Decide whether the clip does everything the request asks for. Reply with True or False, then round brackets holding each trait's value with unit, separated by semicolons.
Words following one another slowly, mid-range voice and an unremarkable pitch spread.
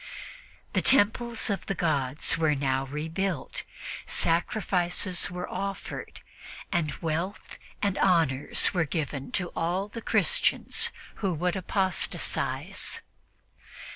True (105 wpm; 175 Hz; 4.1 semitones)